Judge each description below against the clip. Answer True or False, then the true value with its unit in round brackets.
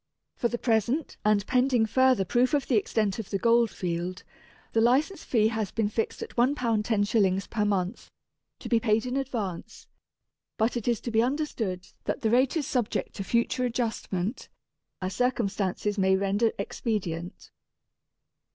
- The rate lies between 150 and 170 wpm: True (160 wpm)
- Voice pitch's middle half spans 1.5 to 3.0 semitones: False (3.6 semitones)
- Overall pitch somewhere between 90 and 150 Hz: False (225 Hz)